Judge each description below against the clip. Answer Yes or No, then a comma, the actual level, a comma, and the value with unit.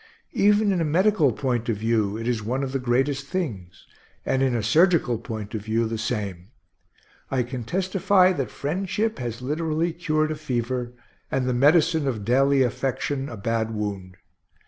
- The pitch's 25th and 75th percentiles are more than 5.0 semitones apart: Yes, wide, 5.4 semitones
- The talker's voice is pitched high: No, low, 130 Hz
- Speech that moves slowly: No, average, 170 wpm